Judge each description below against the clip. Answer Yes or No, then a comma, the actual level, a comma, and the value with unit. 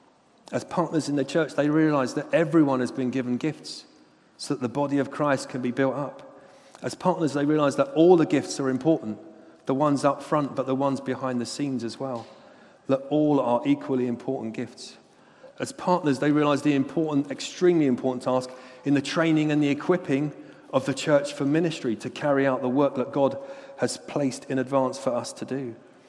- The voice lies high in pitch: No, medium, 140 Hz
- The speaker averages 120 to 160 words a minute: No, average, 200 wpm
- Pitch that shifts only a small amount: Yes, narrow, 2.3 semitones